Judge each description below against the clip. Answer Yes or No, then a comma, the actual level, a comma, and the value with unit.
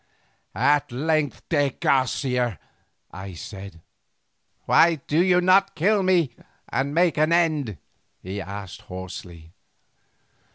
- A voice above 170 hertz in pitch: No, medium, 140 Hz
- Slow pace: Yes, slow, 110 wpm